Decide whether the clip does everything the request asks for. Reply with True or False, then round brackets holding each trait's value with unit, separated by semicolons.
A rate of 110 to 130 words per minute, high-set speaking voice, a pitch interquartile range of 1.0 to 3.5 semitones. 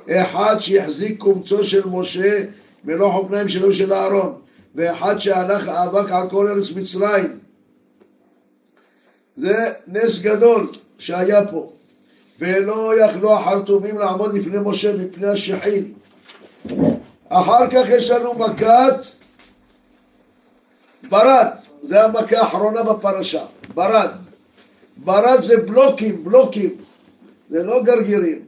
False (100 wpm; 205 Hz; 3.0 semitones)